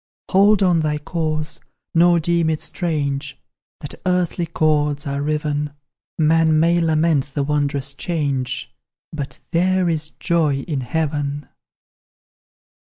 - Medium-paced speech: No, slow, 115 wpm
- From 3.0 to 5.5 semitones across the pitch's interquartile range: No, narrow, 2.6 semitones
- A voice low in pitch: No, medium, 155 Hz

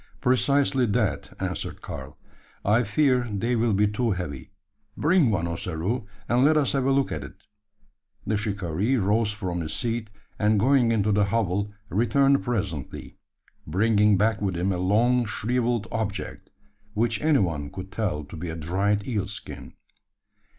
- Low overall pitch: Yes, low, 105 Hz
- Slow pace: No, average, 155 wpm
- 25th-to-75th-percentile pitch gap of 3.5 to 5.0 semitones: Yes, average, 4.4 semitones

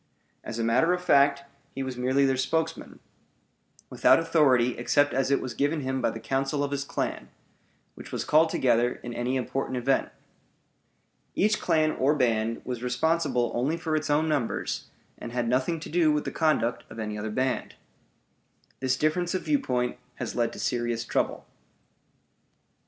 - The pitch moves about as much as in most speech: Yes, average, 4.1 semitones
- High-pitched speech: No, low, 135 Hz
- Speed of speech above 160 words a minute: Yes, average, 170 wpm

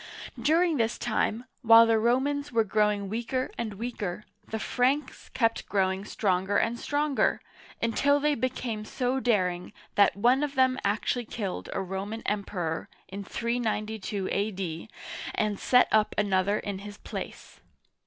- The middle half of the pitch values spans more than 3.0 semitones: Yes, average, 3.7 semitones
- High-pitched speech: Yes, high, 220 Hz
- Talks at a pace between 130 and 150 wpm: Yes, average, 140 wpm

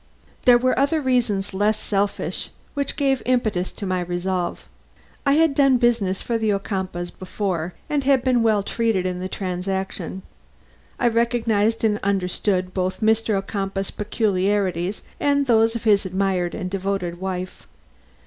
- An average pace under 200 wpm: Yes, average, 140 wpm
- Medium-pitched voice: No, high, 200 Hz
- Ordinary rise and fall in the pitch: Yes, average, 3.8 semitones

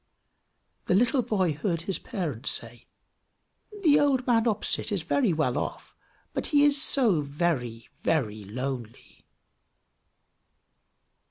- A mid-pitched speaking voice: Yes, medium, 175 Hz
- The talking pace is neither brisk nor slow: No, slow, 115 wpm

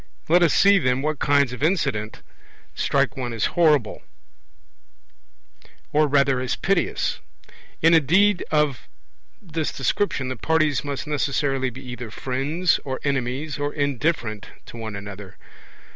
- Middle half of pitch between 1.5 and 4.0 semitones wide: Yes, average, 3.7 semitones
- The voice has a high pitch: No, medium, 140 Hz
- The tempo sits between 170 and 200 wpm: No, slow, 135 wpm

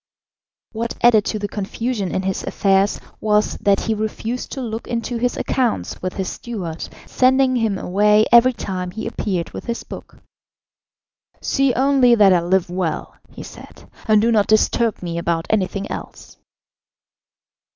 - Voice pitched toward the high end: Yes, high, 215 Hz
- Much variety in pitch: No, average, 3.6 semitones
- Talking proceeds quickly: No, average, 155 wpm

